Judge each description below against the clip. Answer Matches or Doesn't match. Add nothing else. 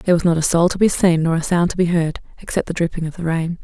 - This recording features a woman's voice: Matches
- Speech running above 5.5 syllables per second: Matches